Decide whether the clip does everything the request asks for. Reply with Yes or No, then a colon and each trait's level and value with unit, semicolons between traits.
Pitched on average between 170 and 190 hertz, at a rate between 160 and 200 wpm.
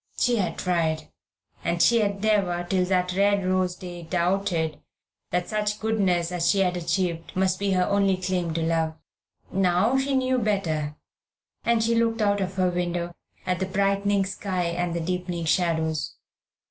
Yes: medium, 185 Hz; average, 165 wpm